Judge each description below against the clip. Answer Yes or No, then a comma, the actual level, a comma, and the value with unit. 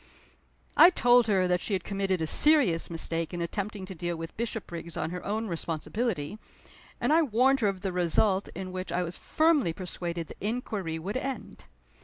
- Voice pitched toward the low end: No, high, 190 Hz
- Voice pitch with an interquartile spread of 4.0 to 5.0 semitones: Yes, average, 4.6 semitones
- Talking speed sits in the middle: Yes, average, 185 wpm